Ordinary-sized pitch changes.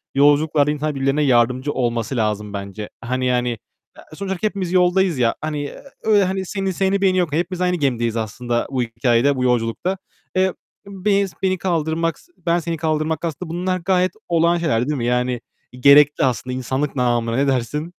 No: wide, 6.3 semitones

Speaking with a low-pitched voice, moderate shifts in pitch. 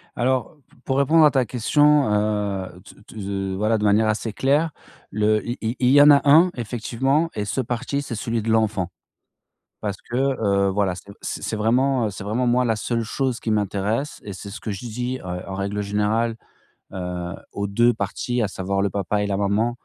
Yes: low, 110 Hz; average, 3.7 semitones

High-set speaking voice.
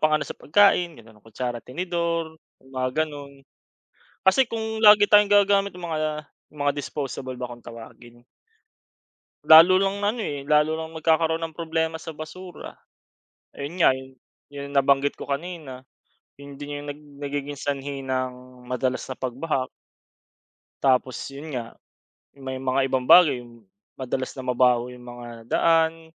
No: medium, 145 Hz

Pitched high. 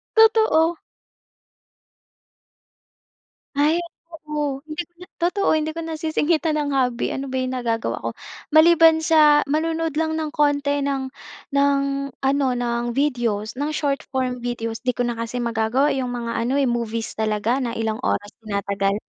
Yes: very high, 275 Hz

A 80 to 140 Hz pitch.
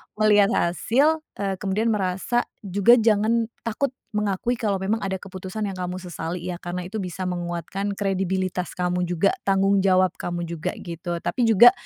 No: high, 190 Hz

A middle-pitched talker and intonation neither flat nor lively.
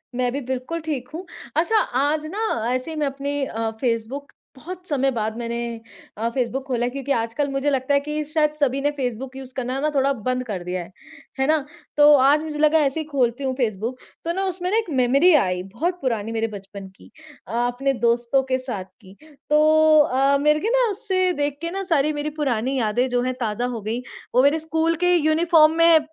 No: very high, 275 Hz; average, 4.0 semitones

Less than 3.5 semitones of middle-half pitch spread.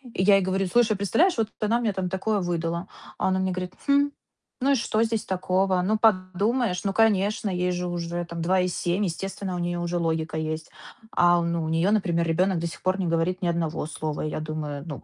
Yes: average, 3.0 semitones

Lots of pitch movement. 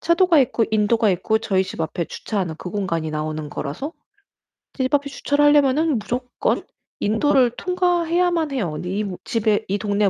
Yes: wide, 7.3 semitones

